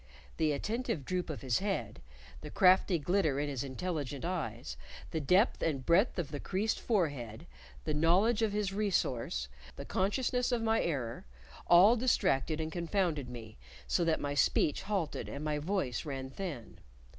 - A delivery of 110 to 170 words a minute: Yes, average, 160 wpm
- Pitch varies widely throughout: Yes, wide, 5.9 semitones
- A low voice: No, medium, 165 Hz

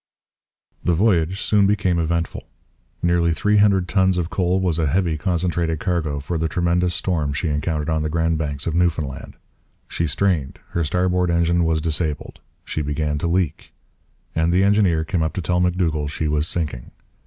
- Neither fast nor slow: Yes, average, 175 wpm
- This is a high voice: No, very low, 85 Hz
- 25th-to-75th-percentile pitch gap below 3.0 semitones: Yes, narrow, 2.4 semitones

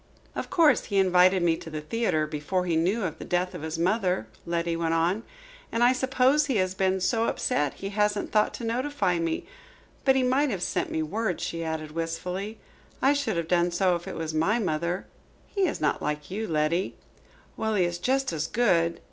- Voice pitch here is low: No, medium, 180 Hz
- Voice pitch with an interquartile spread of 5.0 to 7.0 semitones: Yes, average, 5.3 semitones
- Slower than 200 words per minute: No, fast, 205 wpm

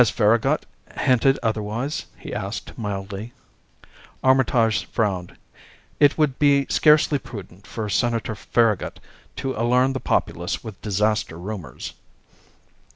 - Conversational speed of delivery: No, slow, 110 wpm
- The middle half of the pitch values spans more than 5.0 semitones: No, average, 4.2 semitones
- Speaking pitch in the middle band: No, low, 115 Hz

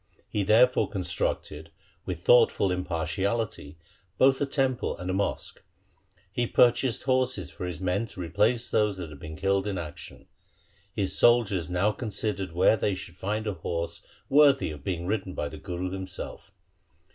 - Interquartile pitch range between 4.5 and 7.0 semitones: Yes, average, 4.8 semitones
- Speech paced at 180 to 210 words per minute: No, average, 160 wpm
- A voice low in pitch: Yes, low, 100 Hz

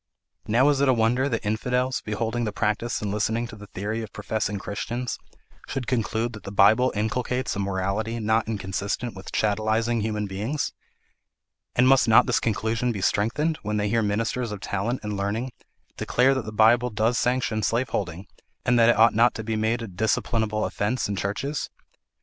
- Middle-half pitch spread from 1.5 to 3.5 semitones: Yes, narrow, 2.6 semitones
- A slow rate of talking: No, average, 180 wpm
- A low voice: Yes, low, 110 Hz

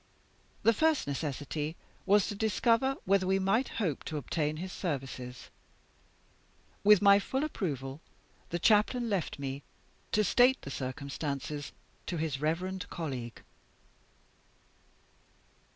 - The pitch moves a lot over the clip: Yes, wide, 6.6 semitones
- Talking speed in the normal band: No, slow, 115 wpm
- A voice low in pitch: No, medium, 175 Hz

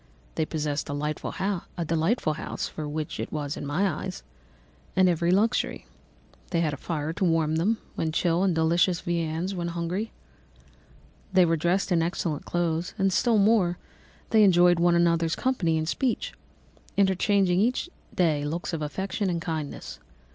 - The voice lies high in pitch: No, medium, 170 Hz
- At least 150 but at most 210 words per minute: Yes, average, 155 wpm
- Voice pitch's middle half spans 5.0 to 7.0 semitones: No, average, 3.0 semitones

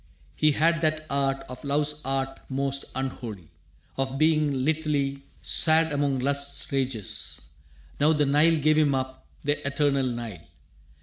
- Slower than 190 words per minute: Yes, slow, 135 wpm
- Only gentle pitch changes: Yes, narrow, 2.1 semitones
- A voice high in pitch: No, medium, 140 Hz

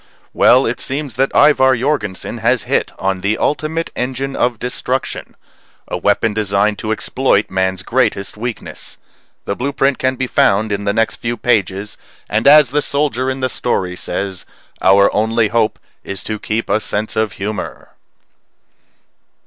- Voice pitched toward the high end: No, low, 115 Hz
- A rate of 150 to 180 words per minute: Yes, average, 155 wpm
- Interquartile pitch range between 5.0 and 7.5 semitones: No, average, 4.4 semitones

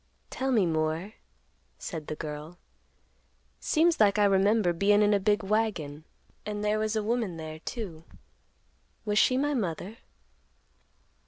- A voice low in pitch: No, high, 205 Hz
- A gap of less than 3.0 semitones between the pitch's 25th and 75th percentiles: No, average, 4.8 semitones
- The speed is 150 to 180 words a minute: No, average, 140 wpm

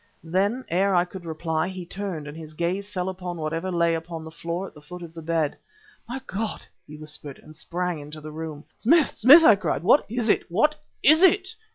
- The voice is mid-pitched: Yes, medium, 175 Hz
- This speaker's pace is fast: Yes, fast, 215 wpm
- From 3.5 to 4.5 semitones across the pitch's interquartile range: Yes, average, 3.9 semitones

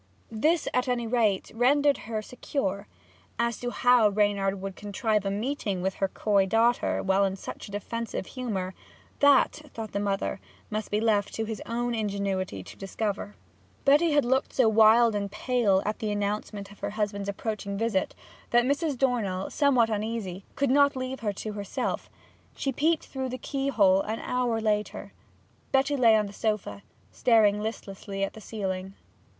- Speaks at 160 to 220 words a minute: Yes, average, 165 wpm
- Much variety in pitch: No, average, 3.6 semitones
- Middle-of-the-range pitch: No, high, 215 Hz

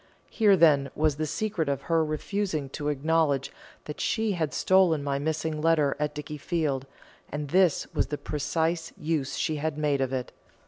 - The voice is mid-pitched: Yes, medium, 155 Hz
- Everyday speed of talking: Yes, average, 170 wpm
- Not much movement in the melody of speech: Yes, narrow, 2.2 semitones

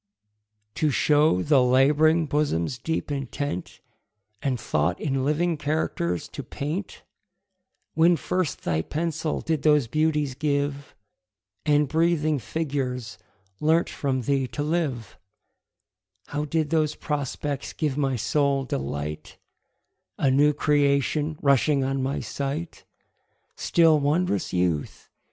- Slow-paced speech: Yes, slow, 115 wpm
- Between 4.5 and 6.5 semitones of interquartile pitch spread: No, average, 2.9 semitones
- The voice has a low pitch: No, medium, 145 Hz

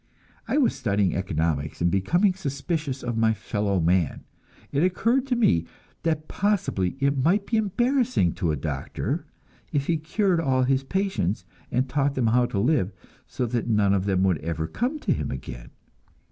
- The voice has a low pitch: Yes, low, 130 Hz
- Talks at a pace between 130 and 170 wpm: No, average, 180 wpm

